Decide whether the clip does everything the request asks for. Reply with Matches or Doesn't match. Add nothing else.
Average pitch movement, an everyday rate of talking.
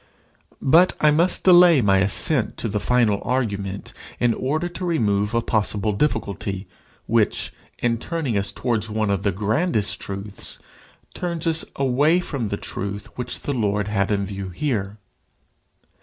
Doesn't match